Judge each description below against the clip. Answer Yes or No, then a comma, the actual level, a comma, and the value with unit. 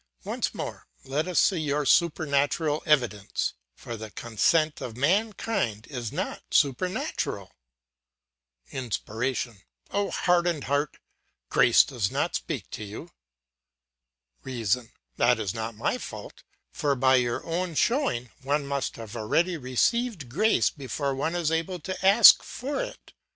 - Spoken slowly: Yes, slow, 130 wpm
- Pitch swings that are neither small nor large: No, wide, 6.2 semitones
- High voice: No, medium, 140 Hz